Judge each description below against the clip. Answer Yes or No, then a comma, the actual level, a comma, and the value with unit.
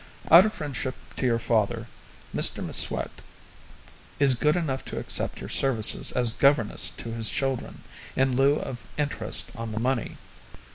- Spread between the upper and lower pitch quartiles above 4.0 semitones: No, average, 3.3 semitones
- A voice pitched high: No, low, 130 Hz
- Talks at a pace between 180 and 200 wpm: No, average, 150 wpm